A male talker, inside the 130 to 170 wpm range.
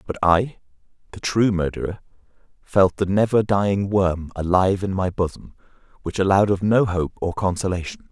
Yes: male; average, 155 wpm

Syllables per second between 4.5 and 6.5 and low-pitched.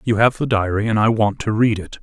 Yes: 5.7 syllables/s; low, 110 Hz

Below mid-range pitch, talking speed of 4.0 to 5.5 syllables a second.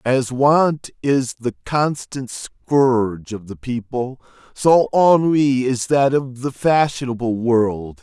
No: low, 130 Hz; 3.4 syllables/s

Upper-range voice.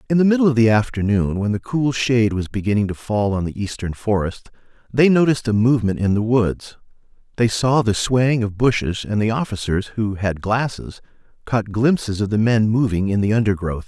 No: low, 110 Hz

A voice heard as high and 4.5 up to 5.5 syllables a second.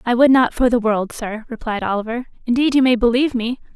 No: high, 240 Hz; 6.1 syllables/s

